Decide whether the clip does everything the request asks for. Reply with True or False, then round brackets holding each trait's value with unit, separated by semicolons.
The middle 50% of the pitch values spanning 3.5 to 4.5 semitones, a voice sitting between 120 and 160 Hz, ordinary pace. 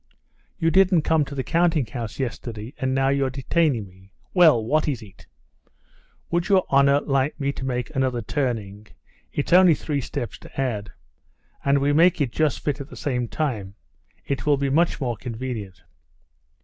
True (4.1 semitones; 135 Hz; 170 wpm)